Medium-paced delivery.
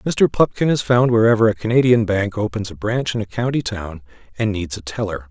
No: fast, 215 wpm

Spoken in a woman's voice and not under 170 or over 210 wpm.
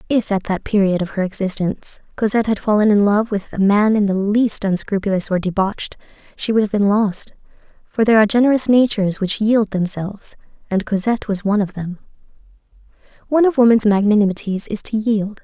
Yes: female; average, 185 wpm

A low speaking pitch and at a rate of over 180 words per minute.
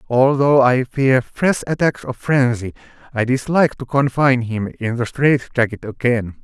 No: low, 130 Hz; average, 160 wpm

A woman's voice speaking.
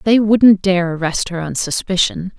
Yes: female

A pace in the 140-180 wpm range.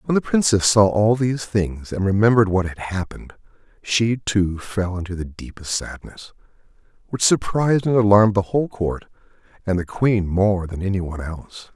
Yes: average, 170 wpm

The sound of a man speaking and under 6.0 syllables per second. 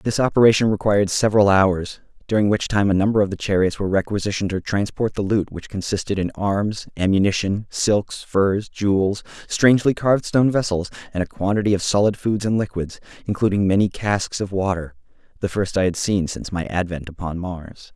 Yes: male; 5.6 syllables/s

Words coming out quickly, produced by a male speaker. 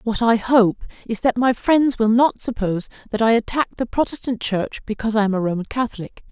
No: fast, 210 wpm; female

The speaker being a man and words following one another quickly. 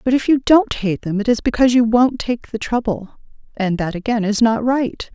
No: female; fast, 235 wpm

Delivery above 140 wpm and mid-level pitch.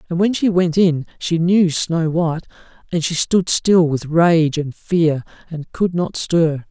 Yes: average, 190 wpm; medium, 165 Hz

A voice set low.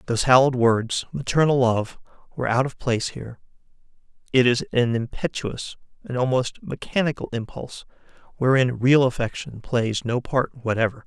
Yes: low, 125 Hz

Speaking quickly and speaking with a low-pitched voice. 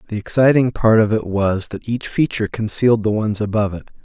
Yes: fast, 210 wpm; low, 110 Hz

